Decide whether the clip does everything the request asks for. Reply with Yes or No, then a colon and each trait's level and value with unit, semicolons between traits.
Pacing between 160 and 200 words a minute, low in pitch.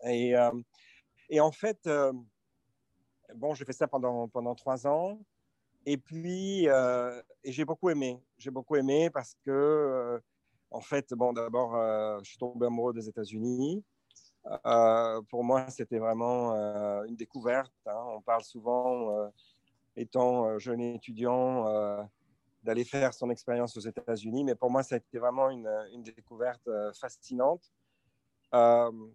No: average, 150 wpm; low, 120 Hz